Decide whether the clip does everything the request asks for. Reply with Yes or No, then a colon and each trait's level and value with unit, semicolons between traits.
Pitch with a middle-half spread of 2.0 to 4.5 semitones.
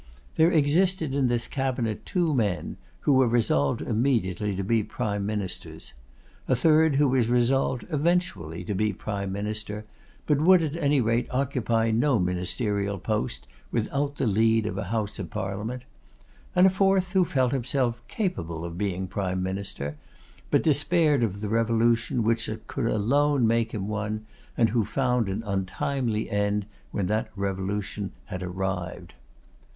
No: average, 5.1 semitones